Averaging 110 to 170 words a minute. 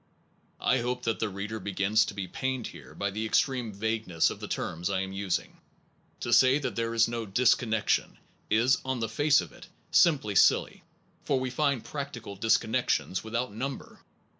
No: average, 180 wpm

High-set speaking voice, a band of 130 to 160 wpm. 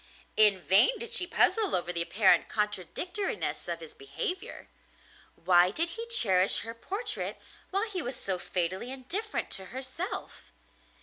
Yes: very high, 260 Hz; average, 140 wpm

